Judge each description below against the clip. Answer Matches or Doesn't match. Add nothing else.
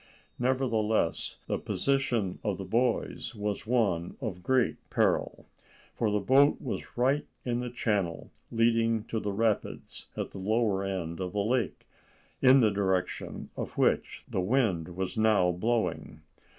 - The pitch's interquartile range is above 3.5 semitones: Matches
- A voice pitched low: Matches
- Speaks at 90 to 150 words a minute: Matches